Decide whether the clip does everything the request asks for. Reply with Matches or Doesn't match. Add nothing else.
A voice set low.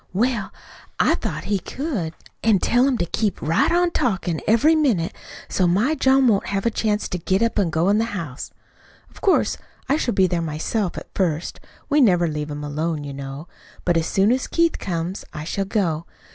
Doesn't match